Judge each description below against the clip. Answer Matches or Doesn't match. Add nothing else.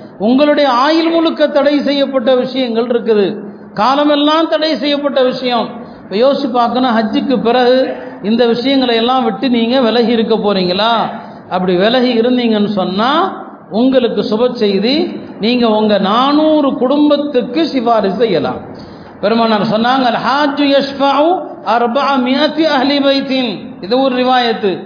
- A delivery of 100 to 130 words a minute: Matches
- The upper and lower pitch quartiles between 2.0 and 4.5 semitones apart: Matches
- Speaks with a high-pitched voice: Matches